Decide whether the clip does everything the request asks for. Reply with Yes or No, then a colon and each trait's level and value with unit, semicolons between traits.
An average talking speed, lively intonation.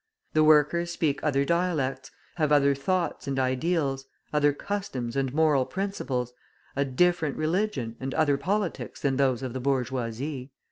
No: average, 145 wpm; average, 3.7 semitones